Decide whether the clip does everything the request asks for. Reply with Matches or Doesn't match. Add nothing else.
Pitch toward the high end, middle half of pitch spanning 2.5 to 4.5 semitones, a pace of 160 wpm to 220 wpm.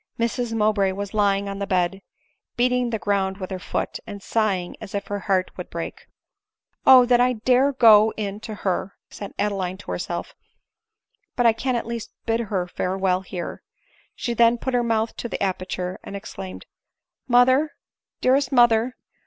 Matches